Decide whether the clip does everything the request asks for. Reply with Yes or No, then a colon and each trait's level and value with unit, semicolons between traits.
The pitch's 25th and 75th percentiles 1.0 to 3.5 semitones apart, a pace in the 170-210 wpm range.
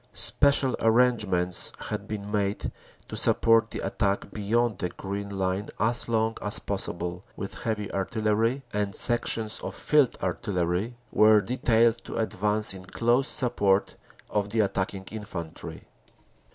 No: average, 2.7 semitones; slow, 135 wpm